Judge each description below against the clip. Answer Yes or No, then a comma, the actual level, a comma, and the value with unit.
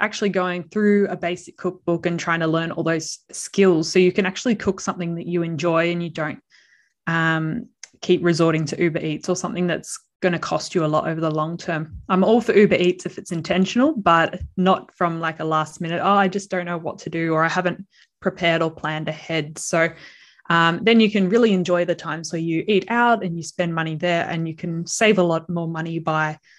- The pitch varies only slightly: Yes, narrow, 2.2 semitones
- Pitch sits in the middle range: Yes, medium, 175 Hz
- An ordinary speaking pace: No, fast, 230 wpm